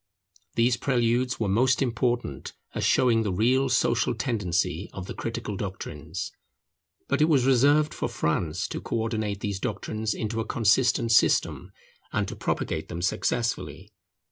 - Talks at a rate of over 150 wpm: No, average, 145 wpm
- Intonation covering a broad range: No, average, 3.8 semitones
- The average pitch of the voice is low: Yes, low, 115 Hz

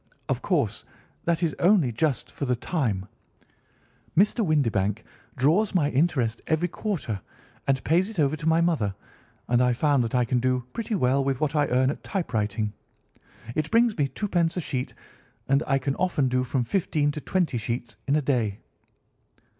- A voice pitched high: No, medium, 140 Hz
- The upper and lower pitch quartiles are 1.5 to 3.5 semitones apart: No, average, 5.1 semitones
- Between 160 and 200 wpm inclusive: Yes, average, 170 wpm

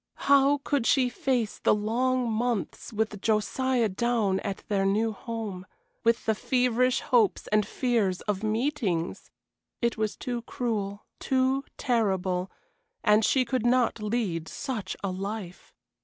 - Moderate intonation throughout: Yes, average, 3.5 semitones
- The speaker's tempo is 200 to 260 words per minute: No, slow, 135 wpm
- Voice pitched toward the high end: Yes, high, 225 Hz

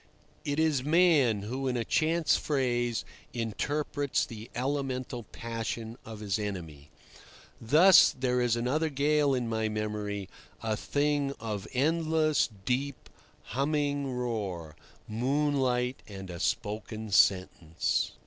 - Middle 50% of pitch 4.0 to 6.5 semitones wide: Yes, average, 4.9 semitones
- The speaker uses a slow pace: Yes, slow, 115 wpm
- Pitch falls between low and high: No, low, 125 Hz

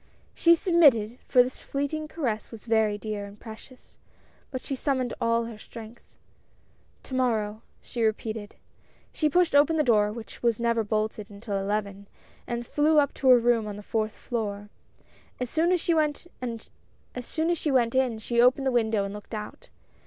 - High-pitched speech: Yes, high, 235 Hz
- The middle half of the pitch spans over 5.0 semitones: No, average, 3.9 semitones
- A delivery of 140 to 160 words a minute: No, average, 170 wpm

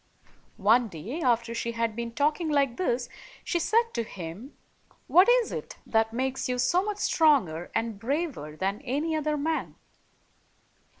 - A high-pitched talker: Yes, very high, 250 Hz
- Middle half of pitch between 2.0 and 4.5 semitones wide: No, wide, 5.5 semitones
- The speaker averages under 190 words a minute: Yes, average, 155 wpm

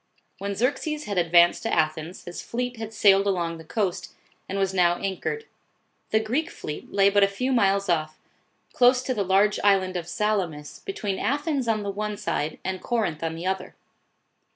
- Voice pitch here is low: No, high, 200 Hz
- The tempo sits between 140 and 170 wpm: No, average, 180 wpm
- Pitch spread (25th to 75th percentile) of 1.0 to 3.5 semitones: No, average, 4.2 semitones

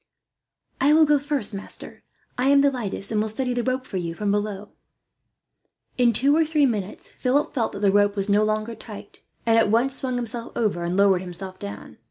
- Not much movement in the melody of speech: No, average, 4.4 semitones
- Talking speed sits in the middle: No, fast, 210 wpm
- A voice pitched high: Yes, high, 220 Hz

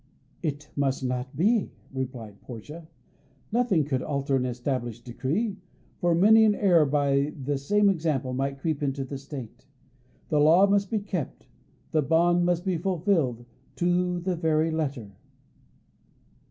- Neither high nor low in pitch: Yes, medium, 150 Hz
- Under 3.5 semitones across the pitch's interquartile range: No, average, 4.7 semitones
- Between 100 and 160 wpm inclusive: Yes, average, 140 wpm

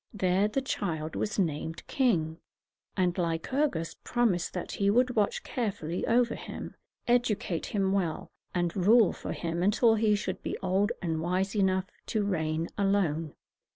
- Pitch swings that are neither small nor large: Yes, average, 4.2 semitones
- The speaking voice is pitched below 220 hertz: Yes, high, 190 Hz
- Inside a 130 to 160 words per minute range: Yes, average, 150 wpm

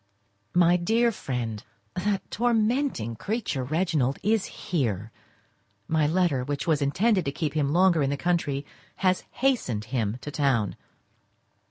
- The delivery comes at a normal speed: No, slow, 130 wpm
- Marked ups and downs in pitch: Yes, wide, 6.0 semitones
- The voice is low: No, medium, 155 Hz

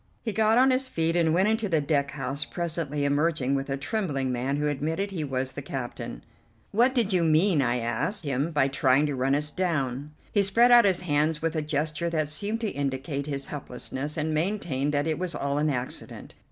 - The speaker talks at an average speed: No, fast, 210 wpm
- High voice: No, medium, 150 Hz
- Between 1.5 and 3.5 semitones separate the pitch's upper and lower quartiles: No, average, 4.4 semitones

